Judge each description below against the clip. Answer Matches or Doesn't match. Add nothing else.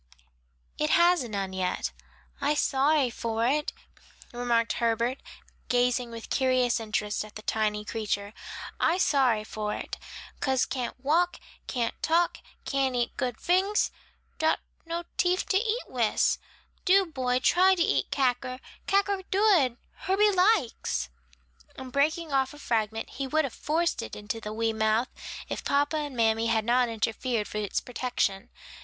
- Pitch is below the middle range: Doesn't match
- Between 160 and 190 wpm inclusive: Doesn't match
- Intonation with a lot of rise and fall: Matches